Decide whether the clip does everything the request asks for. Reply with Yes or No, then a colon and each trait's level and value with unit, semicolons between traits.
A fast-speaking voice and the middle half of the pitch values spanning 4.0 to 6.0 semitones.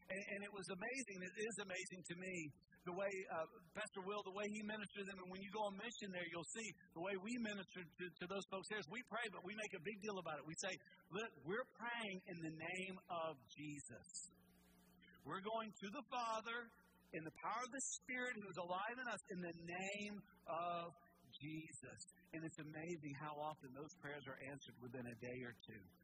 Yes: fast, 220 wpm; average, 4.4 semitones